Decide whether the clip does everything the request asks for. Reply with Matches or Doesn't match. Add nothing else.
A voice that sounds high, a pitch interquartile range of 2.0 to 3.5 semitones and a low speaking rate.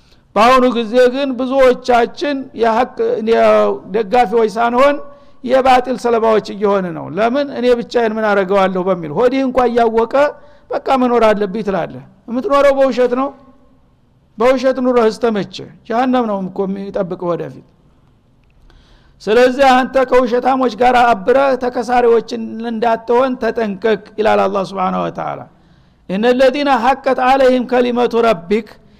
Doesn't match